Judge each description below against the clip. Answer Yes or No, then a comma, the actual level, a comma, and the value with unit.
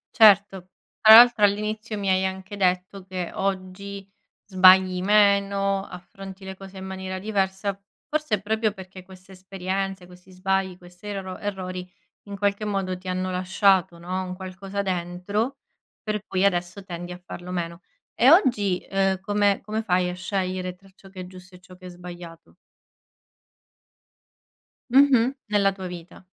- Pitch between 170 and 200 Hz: Yes, high, 190 Hz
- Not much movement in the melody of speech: Yes, narrow, 1.6 semitones